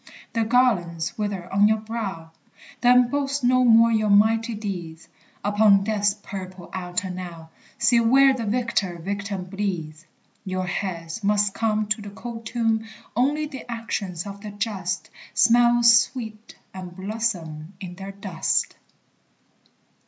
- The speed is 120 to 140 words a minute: Yes, slow, 135 wpm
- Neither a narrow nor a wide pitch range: Yes, average, 3.7 semitones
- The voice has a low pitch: No, high, 205 Hz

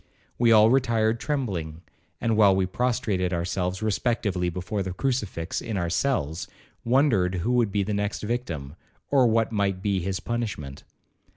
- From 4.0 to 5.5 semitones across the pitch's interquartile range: Yes, average, 4.5 semitones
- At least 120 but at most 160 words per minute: Yes, average, 155 wpm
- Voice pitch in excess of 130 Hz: No, low, 105 Hz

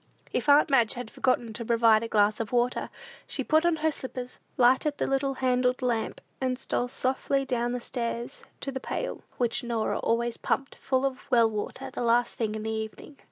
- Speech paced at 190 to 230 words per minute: Yes, average, 195 wpm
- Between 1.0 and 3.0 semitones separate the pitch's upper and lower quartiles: Yes, narrow, 2.5 semitones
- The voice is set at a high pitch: Yes, high, 245 Hz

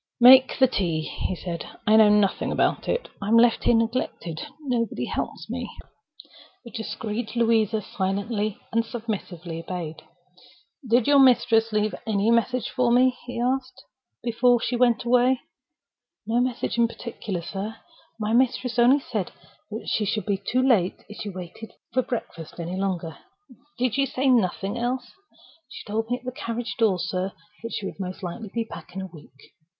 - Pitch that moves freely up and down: No, average, 3.9 semitones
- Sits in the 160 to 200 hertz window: No, high, 225 Hz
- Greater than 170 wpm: No, average, 165 wpm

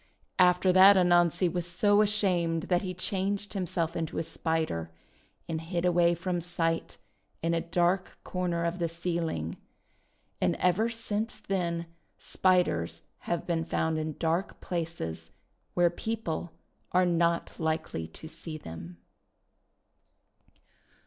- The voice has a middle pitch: Yes, medium, 170 Hz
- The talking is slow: Yes, slow, 125 wpm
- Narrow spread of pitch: Yes, narrow, 2.0 semitones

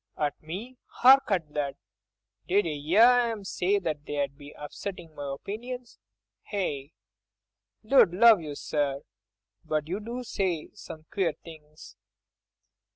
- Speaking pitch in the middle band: Yes, medium, 160 Hz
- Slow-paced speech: Yes, slow, 120 wpm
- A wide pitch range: Yes, wide, 6.1 semitones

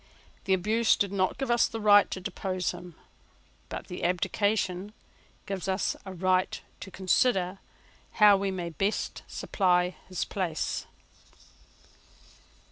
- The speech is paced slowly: Yes, slow, 125 wpm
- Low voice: No, high, 190 Hz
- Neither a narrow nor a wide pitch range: No, narrow, 2.1 semitones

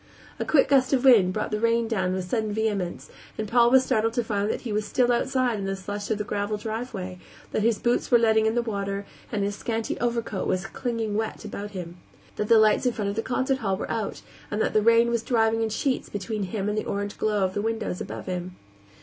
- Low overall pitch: No, high, 215 Hz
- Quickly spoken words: Yes, fast, 245 wpm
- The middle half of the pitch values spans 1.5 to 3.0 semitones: Yes, narrow, 2.4 semitones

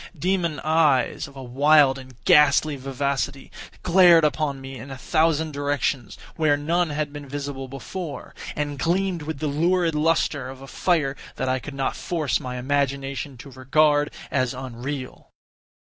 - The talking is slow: No, average, 155 wpm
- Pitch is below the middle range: No, medium, 145 Hz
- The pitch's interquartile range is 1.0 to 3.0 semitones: Yes, narrow, 2.6 semitones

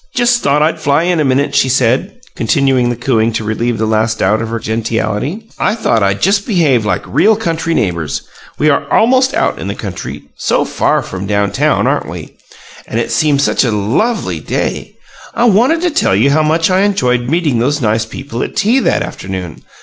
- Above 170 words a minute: Yes, fast, 205 wpm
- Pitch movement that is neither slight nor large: No, wide, 8.3 semitones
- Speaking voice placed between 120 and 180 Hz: Yes, low, 135 Hz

